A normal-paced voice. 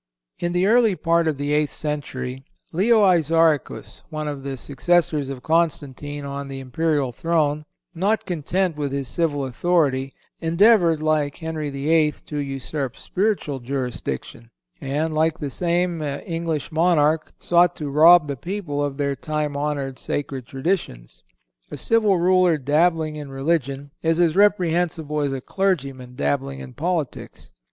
Yes: average, 145 wpm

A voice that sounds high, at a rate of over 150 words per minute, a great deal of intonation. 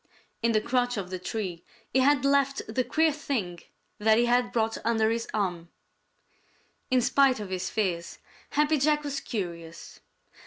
Yes: high, 230 Hz; average, 160 wpm; wide, 6.1 semitones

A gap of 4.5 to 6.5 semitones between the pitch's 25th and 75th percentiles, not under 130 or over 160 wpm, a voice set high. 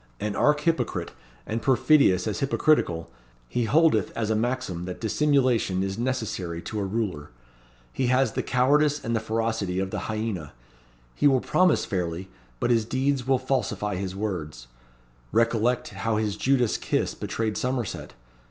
No: average, 5.0 semitones; average, 150 wpm; low, 115 Hz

